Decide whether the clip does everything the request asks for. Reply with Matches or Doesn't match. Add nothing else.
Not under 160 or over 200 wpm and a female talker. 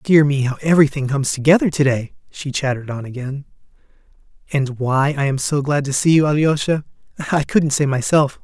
Doesn't match